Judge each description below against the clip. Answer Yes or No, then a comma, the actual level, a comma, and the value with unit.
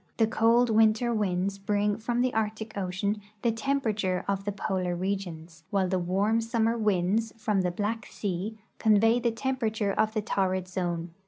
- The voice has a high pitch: Yes, high, 210 Hz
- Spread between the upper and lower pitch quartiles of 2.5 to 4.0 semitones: Yes, average, 3.1 semitones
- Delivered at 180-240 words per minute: No, average, 165 wpm